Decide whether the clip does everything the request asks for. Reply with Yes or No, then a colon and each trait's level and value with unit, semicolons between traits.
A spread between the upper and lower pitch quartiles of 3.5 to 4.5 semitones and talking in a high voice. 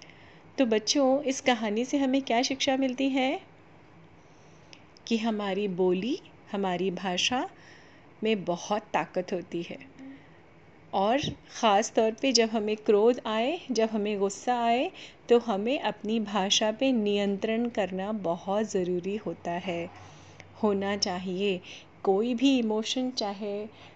Yes: average, 4.2 semitones; high, 215 Hz